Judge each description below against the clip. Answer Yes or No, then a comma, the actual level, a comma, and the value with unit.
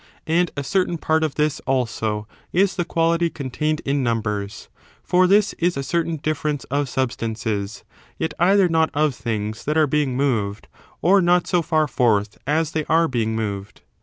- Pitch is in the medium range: Yes, medium, 150 Hz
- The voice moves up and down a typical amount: No, wide, 6.3 semitones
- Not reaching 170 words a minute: No, average, 175 wpm